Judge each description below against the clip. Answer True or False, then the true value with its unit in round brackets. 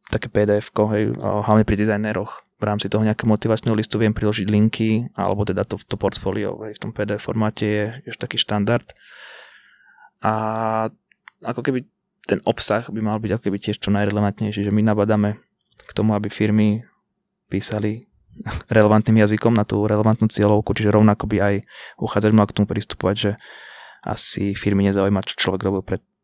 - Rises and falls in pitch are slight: True (1.0 semitones)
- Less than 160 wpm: False (165 wpm)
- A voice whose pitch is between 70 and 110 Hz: True (105 Hz)